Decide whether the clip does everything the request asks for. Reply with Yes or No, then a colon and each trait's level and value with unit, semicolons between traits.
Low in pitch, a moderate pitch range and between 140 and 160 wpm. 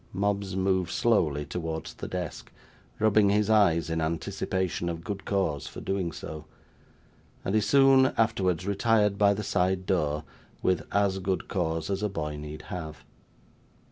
Yes: very low, 95 Hz; average, 3.7 semitones; average, 150 wpm